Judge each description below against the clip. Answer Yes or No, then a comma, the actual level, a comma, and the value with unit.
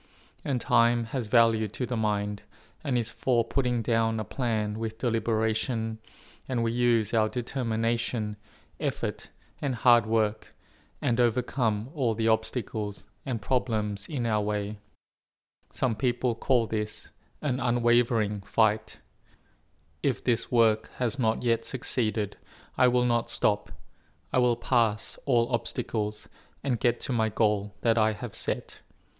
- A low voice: Yes, low, 115 Hz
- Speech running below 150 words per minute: Yes, average, 140 wpm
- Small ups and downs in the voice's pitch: Yes, narrow, 2.3 semitones